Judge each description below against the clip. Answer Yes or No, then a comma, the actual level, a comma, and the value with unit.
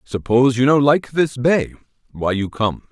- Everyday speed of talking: Yes, average, 185 wpm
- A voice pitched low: Yes, low, 130 Hz